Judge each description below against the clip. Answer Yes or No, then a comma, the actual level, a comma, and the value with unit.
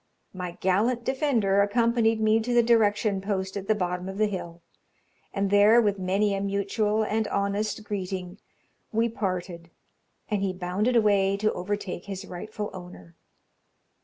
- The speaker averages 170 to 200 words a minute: No, average, 150 wpm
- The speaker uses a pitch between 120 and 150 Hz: No, high, 200 Hz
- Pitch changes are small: Yes, narrow, 2.3 semitones